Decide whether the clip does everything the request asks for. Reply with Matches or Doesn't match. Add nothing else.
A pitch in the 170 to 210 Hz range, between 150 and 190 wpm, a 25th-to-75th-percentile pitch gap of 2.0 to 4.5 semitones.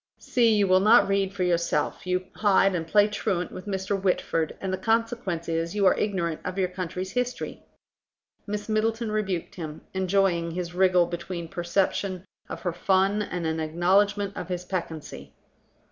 Matches